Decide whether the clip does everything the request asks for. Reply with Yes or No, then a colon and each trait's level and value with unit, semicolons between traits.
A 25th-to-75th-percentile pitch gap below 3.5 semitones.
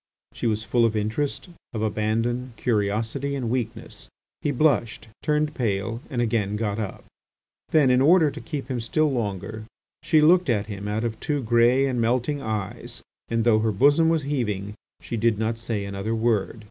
No: average, 4.0 semitones